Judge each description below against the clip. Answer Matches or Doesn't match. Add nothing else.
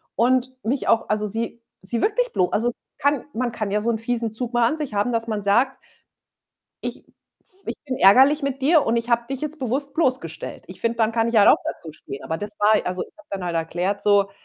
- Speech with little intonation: Doesn't match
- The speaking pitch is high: Matches